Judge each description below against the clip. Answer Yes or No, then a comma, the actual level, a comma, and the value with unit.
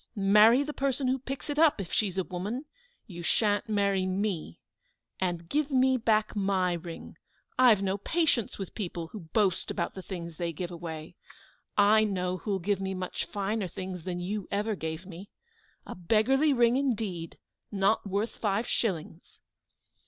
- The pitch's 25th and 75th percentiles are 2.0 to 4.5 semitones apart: Yes, average, 3.8 semitones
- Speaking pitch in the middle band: No, high, 200 Hz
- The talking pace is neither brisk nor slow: Yes, average, 165 wpm